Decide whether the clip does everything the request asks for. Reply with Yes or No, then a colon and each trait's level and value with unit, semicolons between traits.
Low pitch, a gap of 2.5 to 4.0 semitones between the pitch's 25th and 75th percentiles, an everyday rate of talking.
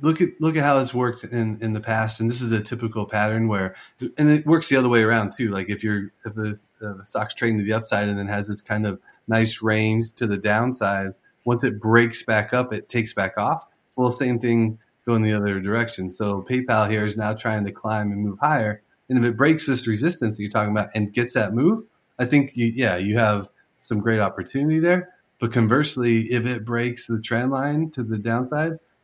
No: low, 115 Hz; average, 2.9 semitones; fast, 225 wpm